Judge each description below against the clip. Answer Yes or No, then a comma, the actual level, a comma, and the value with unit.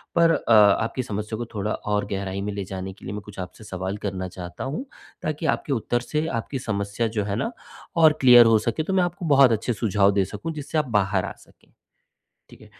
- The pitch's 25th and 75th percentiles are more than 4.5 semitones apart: Yes, wide, 5.4 semitones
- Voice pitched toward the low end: Yes, low, 105 Hz